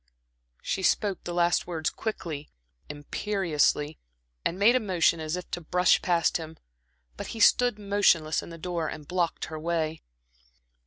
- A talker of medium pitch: Yes, medium, 170 Hz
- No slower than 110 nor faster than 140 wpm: No, average, 155 wpm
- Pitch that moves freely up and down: No, average, 3.3 semitones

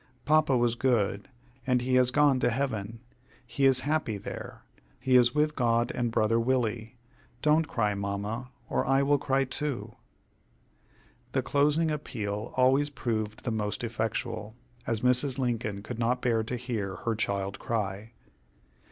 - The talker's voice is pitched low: Yes, low, 120 Hz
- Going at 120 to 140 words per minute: No, average, 150 wpm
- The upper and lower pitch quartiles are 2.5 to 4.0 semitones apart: Yes, average, 3.3 semitones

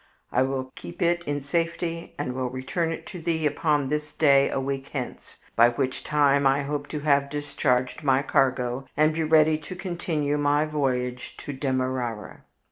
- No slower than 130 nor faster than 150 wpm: No, average, 175 wpm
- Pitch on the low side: No, medium, 145 Hz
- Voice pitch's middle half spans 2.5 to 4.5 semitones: Yes, average, 2.8 semitones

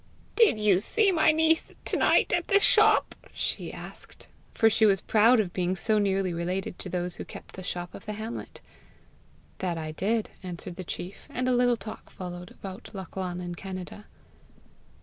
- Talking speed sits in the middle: Yes, average, 180 wpm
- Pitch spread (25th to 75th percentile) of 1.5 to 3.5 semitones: No, average, 4.0 semitones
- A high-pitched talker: Yes, high, 195 Hz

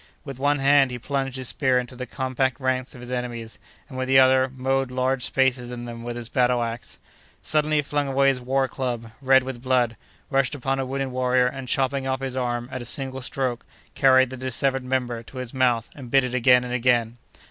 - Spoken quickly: Yes, fast, 220 wpm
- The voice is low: Yes, low, 130 Hz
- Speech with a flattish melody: Yes, narrow, 1.5 semitones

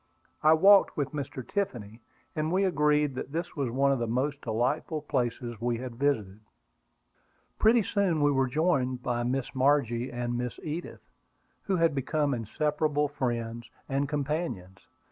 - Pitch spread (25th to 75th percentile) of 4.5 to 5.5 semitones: No, average, 4.0 semitones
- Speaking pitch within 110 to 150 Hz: Yes, medium, 140 Hz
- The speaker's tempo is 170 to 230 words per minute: No, average, 150 wpm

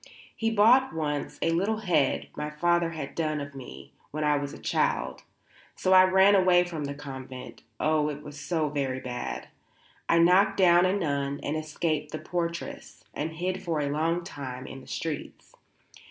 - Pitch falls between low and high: Yes, medium, 155 Hz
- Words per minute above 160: Yes, average, 175 wpm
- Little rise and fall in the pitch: No, average, 3.6 semitones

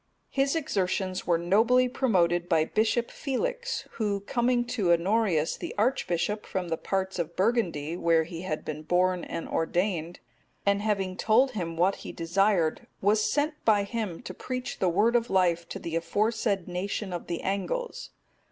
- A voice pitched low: No, high, 195 Hz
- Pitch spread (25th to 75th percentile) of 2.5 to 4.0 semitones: No, average, 4.9 semitones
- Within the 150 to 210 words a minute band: Yes, average, 160 wpm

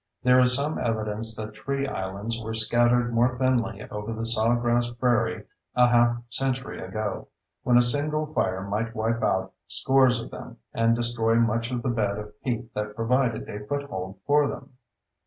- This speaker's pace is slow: No, average, 170 wpm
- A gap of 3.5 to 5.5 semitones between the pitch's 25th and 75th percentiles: No, narrow, 2.4 semitones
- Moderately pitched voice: No, low, 115 Hz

